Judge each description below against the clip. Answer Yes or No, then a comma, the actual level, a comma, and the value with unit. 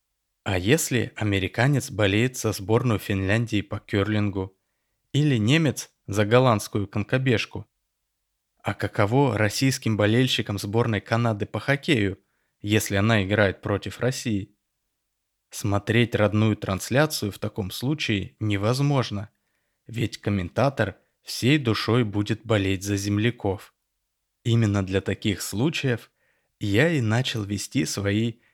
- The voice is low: Yes, low, 110 Hz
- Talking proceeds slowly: Yes, slow, 105 wpm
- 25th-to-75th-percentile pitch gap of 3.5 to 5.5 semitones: No, average, 3.1 semitones